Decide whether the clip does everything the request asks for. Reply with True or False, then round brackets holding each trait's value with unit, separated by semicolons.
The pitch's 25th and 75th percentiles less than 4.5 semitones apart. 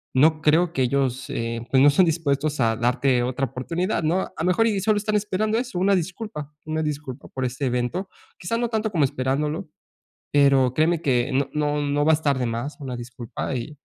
False (5.2 semitones)